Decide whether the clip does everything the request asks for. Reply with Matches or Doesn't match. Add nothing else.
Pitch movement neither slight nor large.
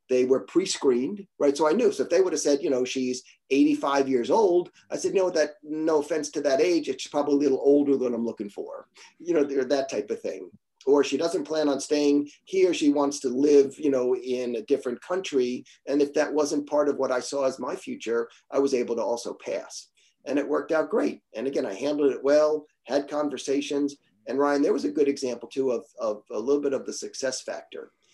Doesn't match